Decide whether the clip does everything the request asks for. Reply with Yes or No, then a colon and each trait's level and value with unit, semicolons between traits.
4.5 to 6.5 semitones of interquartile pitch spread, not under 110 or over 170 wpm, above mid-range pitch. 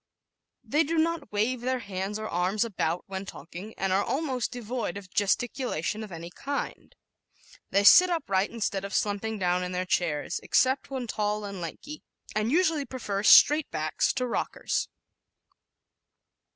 Yes: average, 5.2 semitones; average, 150 wpm; high, 210 Hz